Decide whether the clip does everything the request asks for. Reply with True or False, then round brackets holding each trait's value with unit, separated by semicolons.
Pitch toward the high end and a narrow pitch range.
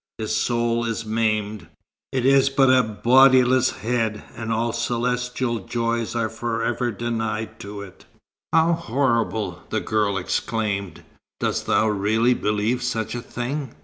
False (115 Hz; 2.3 semitones)